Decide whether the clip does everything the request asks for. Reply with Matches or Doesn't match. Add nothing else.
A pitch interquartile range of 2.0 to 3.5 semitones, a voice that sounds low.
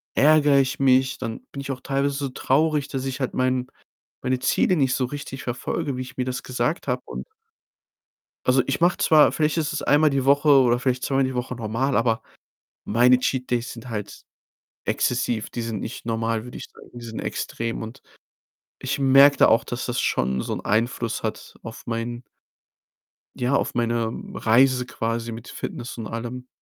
Matches